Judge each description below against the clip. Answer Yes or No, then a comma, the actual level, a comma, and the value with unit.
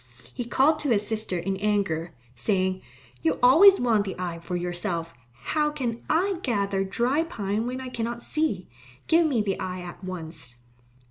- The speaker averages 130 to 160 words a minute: No, average, 170 wpm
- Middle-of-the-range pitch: No, high, 205 Hz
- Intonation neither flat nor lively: No, wide, 6.0 semitones